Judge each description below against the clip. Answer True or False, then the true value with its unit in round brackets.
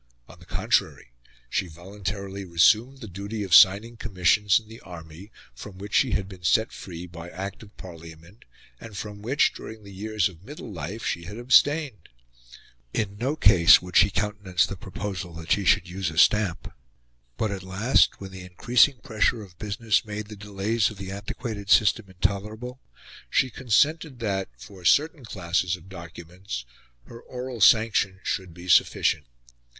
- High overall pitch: False (100 Hz)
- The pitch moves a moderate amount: True (3.4 semitones)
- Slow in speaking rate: False (165 wpm)